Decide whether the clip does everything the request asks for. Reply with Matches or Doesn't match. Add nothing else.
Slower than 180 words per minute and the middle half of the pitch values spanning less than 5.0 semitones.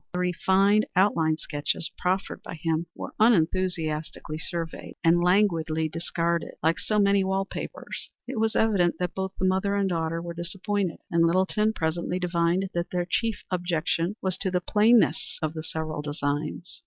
Matches